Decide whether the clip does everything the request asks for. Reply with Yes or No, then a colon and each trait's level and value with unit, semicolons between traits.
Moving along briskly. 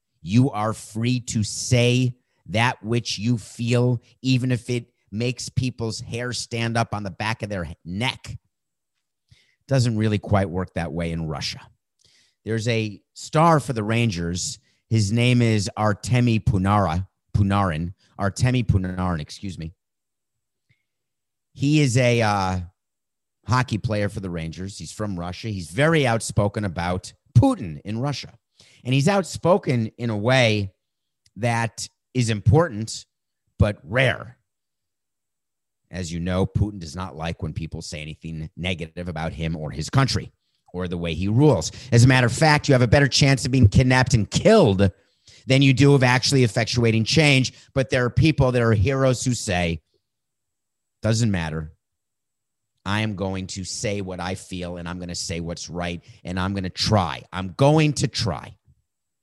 No: average, 160 wpm